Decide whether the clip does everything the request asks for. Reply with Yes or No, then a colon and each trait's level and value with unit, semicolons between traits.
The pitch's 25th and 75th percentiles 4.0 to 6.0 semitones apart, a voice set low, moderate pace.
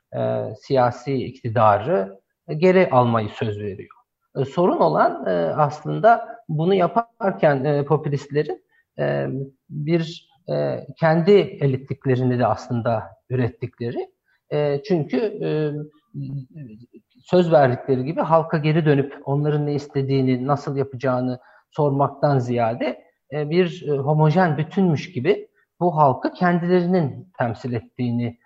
No: average, 5.1 semitones; medium, 145 Hz; average, 110 wpm